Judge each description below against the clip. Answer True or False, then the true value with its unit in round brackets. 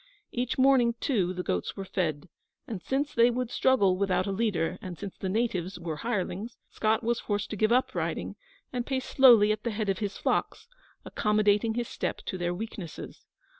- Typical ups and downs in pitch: True (4.1 semitones)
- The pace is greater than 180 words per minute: True (190 wpm)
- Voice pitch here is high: True (215 Hz)